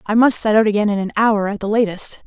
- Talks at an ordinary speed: No, fast, 290 wpm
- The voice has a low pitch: No, high, 210 Hz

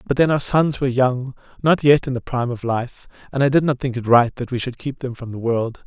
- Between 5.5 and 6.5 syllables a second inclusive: Yes, 5.8 syllables/s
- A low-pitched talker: Yes, low, 130 Hz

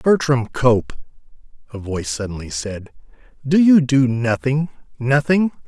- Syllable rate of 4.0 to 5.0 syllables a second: Yes, 4.3 syllables/s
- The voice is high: No, low, 130 Hz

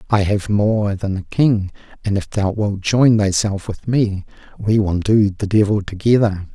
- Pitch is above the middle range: No, low, 105 Hz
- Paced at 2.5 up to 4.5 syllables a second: Yes, 4.3 syllables/s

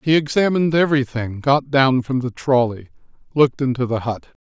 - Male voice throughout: Yes, male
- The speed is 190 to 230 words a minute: No, average, 160 wpm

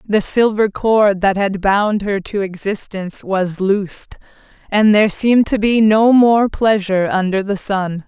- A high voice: Yes, high, 205 Hz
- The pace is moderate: Yes, average, 165 wpm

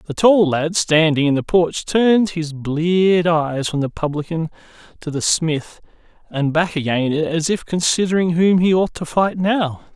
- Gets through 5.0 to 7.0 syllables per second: No, 4.3 syllables/s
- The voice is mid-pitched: Yes, medium, 165 Hz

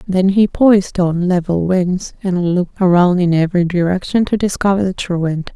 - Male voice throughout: No, female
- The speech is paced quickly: No, average, 175 wpm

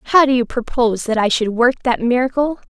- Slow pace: No, fast, 220 wpm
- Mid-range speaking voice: No, high, 245 Hz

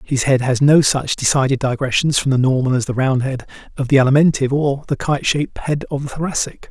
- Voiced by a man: Yes, male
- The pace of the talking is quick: Yes, fast, 225 wpm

